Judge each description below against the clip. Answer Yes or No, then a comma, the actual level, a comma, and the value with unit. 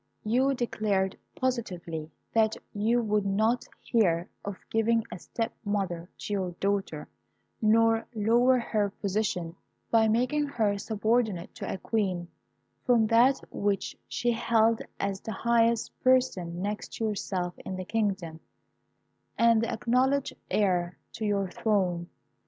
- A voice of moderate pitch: No, high, 215 Hz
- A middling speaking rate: No, slow, 130 wpm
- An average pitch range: Yes, average, 3.2 semitones